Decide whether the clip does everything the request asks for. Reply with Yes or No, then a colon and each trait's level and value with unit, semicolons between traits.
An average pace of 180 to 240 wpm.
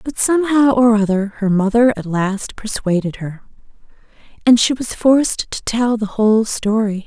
No: average, 160 wpm